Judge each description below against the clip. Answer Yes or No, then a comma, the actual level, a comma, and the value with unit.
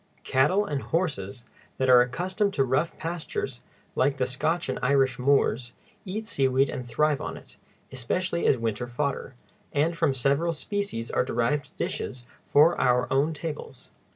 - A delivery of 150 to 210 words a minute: Yes, average, 155 wpm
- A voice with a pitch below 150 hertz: Yes, medium, 140 Hz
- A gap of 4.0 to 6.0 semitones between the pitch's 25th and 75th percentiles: Yes, average, 4.5 semitones